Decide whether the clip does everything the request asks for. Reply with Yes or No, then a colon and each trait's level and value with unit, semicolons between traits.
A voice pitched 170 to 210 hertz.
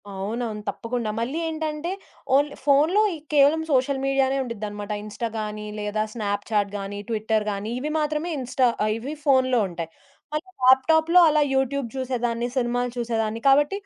No: high, 245 Hz